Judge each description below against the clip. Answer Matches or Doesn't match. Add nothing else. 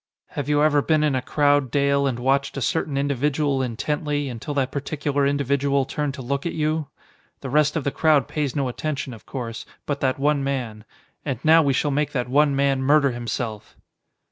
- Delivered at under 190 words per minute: Doesn't match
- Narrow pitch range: Matches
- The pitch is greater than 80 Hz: Matches